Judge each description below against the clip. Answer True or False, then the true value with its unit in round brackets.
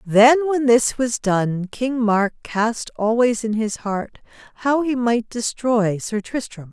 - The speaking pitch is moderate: False (230 Hz)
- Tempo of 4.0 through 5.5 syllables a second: False (3.5 syllables/s)